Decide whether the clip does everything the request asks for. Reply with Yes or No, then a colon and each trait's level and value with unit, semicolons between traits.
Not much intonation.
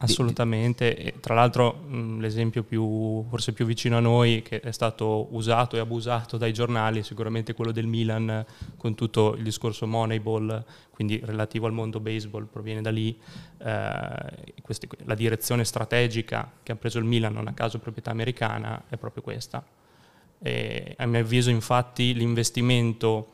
Yes: narrow, 1.4 semitones